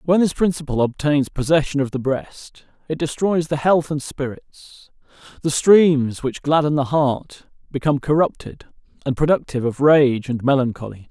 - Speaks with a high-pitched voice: No, medium, 145 Hz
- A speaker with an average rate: Yes, average, 150 wpm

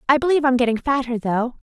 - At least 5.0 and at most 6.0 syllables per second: No, 7.1 syllables/s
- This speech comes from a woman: Yes, female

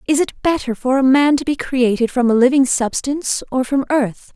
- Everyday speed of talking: No, fast, 220 wpm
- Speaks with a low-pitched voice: No, very high, 260 Hz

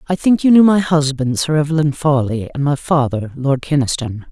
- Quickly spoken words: No, average, 195 wpm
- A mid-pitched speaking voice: Yes, medium, 145 Hz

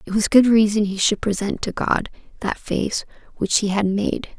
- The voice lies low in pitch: No, high, 205 Hz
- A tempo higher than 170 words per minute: Yes, fast, 205 wpm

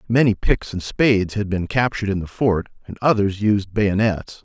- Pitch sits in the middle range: No, low, 105 Hz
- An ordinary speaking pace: Yes, average, 190 wpm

